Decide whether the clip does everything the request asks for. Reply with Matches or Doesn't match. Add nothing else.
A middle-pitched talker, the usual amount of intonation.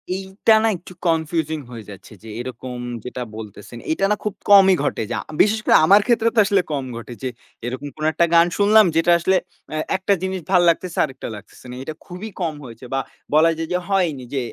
Doesn't match